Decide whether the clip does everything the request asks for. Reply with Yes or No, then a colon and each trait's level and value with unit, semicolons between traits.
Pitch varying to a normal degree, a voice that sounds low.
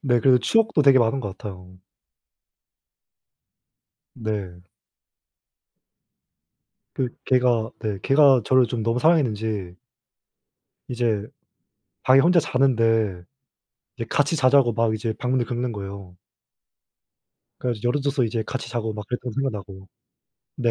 Yes: average, 3.5 semitones; low, 120 Hz